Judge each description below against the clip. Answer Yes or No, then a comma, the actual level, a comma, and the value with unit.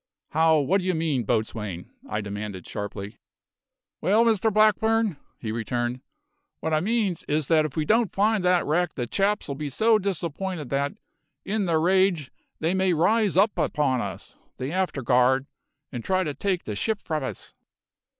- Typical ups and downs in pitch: No, wide, 6.9 semitones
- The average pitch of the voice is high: No, medium, 160 Hz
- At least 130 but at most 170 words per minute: Yes, average, 160 wpm